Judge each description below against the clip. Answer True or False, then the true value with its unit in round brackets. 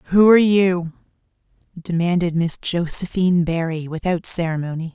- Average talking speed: False (110 wpm)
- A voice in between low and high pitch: True (175 Hz)